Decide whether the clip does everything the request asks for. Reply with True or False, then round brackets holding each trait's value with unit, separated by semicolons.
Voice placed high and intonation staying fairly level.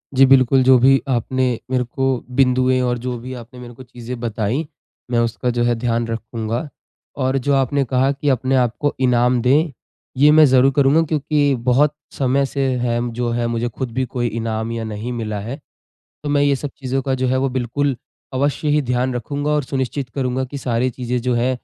False (130 Hz; 2.2 semitones)